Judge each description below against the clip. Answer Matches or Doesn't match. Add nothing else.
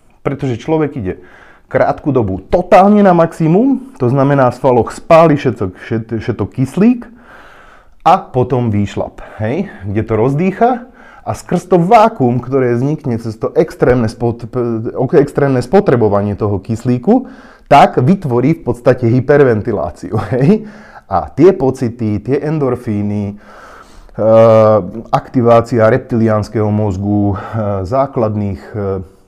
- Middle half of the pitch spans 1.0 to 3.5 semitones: Doesn't match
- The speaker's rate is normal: Doesn't match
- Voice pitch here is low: Matches